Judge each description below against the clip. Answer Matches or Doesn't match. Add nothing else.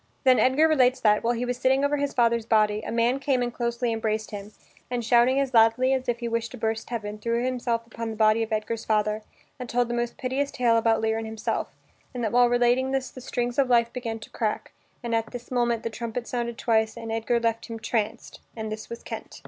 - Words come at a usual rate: Doesn't match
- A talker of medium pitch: Doesn't match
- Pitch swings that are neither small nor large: Doesn't match